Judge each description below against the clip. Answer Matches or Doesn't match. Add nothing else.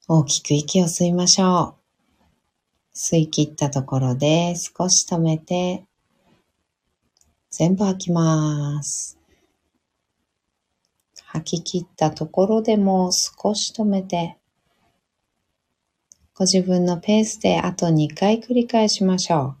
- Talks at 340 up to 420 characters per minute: Doesn't match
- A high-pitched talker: Doesn't match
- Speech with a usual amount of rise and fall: Matches